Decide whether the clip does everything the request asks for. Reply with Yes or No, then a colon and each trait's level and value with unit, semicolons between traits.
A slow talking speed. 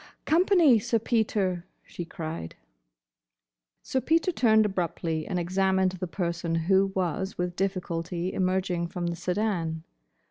Yes: slow, 120 wpm